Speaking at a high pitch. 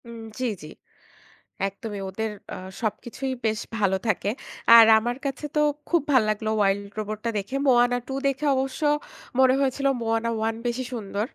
Yes: high, 230 Hz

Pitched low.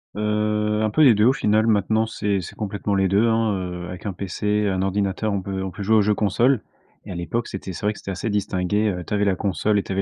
Yes: low, 105 Hz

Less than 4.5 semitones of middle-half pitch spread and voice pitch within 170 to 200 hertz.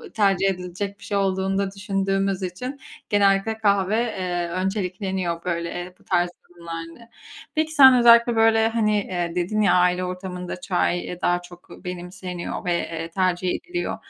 Yes: narrow, 2.5 semitones; high, 190 Hz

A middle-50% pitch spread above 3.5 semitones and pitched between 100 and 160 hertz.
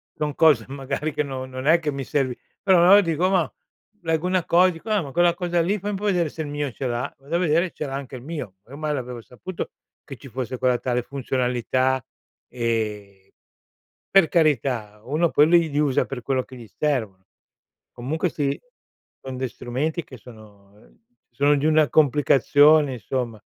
Yes: average, 4.4 semitones; medium, 140 Hz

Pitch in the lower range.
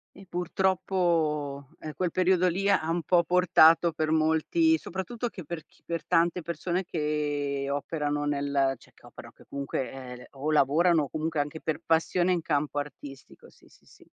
No: medium, 160 Hz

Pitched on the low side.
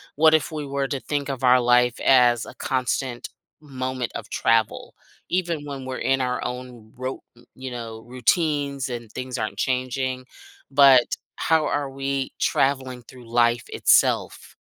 Yes: low, 130 Hz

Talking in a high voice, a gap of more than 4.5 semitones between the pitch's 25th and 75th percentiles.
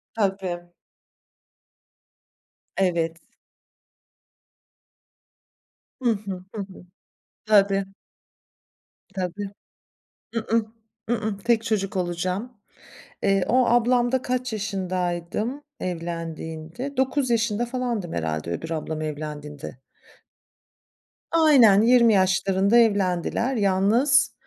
Yes: high, 200 Hz; average, 5.1 semitones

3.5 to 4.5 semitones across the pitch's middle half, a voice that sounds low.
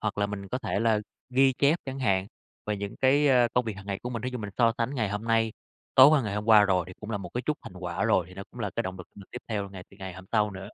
Yes: average, 4.1 semitones; low, 105 Hz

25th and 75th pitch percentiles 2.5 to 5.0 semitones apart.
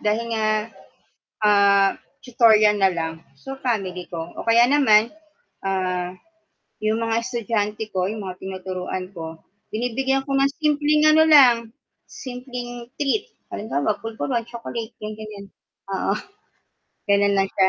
Yes: average, 4.2 semitones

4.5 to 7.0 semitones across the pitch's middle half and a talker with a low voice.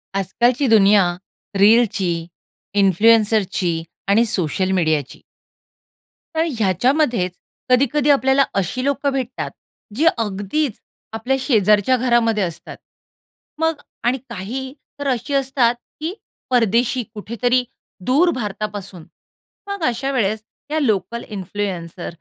No: average, 4.9 semitones; high, 230 Hz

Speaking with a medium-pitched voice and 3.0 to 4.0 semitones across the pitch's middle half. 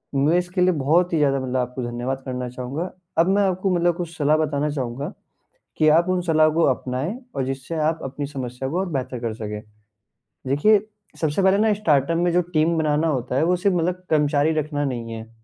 No: medium, 150 Hz; average, 4.6 semitones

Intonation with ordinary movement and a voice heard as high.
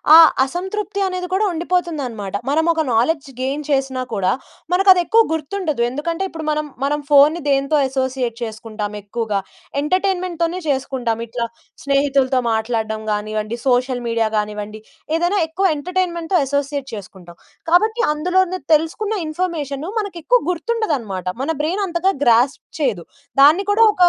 No: wide, 7.0 semitones; very high, 290 Hz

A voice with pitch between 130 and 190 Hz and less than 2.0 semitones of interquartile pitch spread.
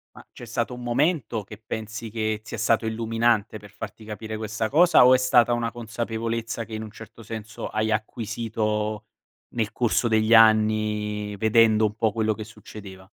No: low, 110 Hz; narrow, 1.3 semitones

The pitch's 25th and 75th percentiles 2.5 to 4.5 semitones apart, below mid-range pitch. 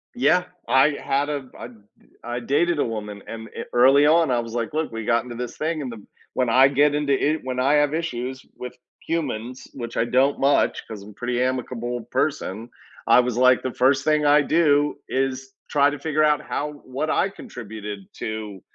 Yes: average, 3.6 semitones; low, 130 Hz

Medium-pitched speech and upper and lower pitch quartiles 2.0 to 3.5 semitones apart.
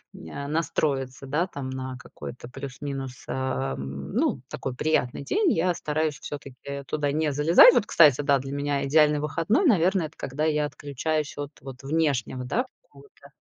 Yes: medium, 145 Hz; average, 3.0 semitones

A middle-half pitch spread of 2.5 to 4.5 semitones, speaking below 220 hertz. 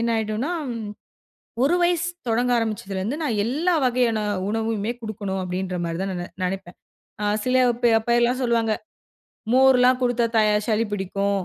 No: average, 3.8 semitones; high, 225 Hz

